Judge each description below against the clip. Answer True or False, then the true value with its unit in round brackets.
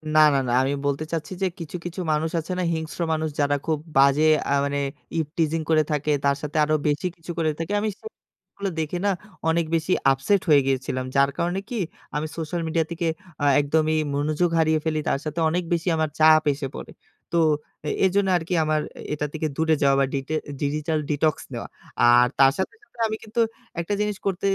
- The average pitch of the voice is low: False (155 Hz)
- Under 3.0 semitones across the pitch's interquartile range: True (2.6 semitones)